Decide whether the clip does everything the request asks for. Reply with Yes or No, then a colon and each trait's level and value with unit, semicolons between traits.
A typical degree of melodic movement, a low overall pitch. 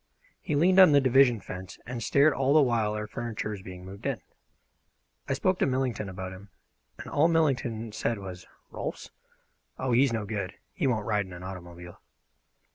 No: wide, 5.7 semitones; low, 115 Hz